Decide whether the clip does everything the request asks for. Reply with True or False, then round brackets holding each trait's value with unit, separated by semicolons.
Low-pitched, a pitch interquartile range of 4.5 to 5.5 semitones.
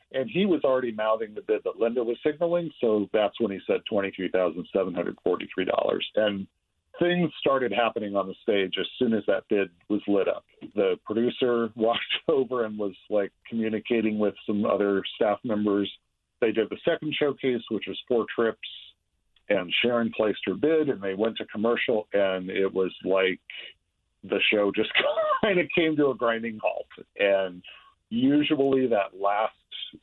True (110 Hz; 5.2 semitones)